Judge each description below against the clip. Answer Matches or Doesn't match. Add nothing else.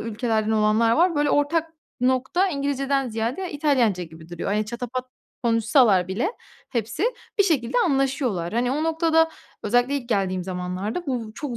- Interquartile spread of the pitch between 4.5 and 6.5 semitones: Matches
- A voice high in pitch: Matches